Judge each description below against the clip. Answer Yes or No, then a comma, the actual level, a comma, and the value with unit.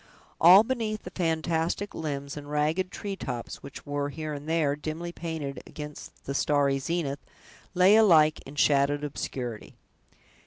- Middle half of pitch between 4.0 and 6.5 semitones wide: No, average, 3.3 semitones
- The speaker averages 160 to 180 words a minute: No, average, 145 wpm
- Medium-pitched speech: Yes, medium, 150 Hz